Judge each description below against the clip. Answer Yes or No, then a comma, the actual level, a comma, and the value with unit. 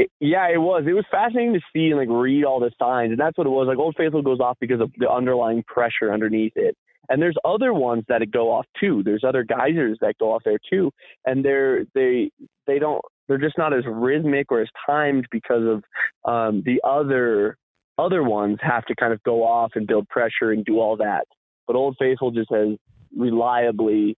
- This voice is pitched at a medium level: No, low, 125 Hz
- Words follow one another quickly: Yes, fast, 215 wpm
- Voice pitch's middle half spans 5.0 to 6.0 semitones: Yes, wide, 5.4 semitones